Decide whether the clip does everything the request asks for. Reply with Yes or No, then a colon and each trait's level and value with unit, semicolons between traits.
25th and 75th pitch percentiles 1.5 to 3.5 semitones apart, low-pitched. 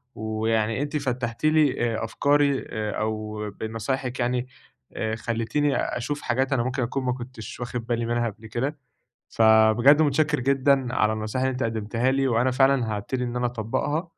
Yes: average, 3.2 semitones; low, 120 Hz